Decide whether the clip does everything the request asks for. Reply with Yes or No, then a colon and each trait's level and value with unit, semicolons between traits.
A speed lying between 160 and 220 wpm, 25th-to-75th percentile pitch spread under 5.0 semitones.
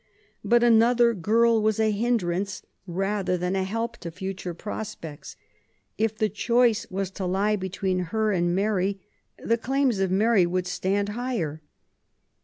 No: average, 145 wpm; average, 3.5 semitones